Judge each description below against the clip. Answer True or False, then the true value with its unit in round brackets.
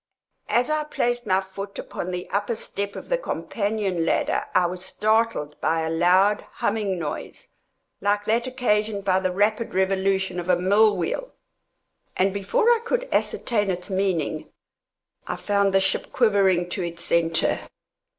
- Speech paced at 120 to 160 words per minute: True (155 wpm)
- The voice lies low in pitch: False (195 Hz)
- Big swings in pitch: False (3.0 semitones)